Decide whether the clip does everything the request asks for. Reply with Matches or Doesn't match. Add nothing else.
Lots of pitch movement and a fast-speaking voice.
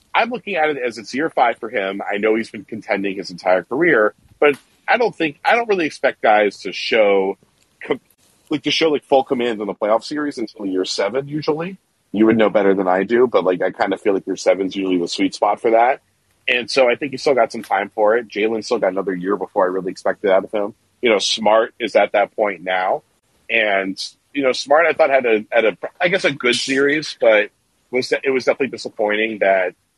Matches